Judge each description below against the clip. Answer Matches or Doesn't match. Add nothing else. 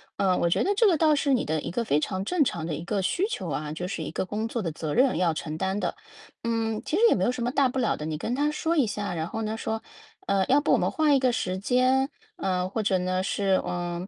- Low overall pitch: Doesn't match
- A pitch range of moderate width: Doesn't match